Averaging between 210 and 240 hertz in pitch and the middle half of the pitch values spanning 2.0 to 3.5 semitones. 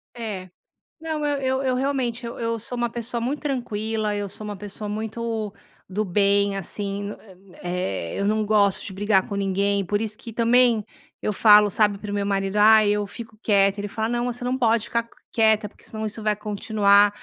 Yes: high, 215 Hz; narrow, 2.5 semitones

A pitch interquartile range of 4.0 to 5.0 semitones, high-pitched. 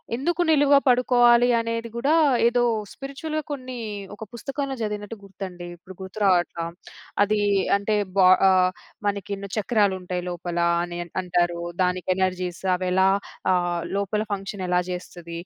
Yes: average, 4.7 semitones; high, 200 Hz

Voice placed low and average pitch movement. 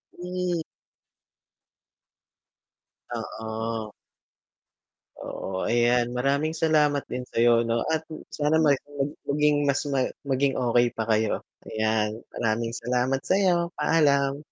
Yes: low, 130 Hz; average, 4.4 semitones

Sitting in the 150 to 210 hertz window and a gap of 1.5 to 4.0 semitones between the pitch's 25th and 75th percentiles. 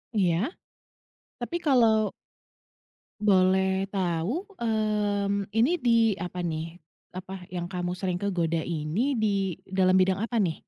Yes: high, 190 Hz; average, 3.4 semitones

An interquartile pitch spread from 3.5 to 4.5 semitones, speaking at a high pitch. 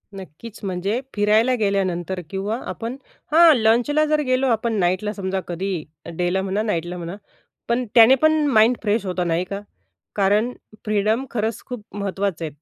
Yes: average, 3.8 semitones; high, 210 Hz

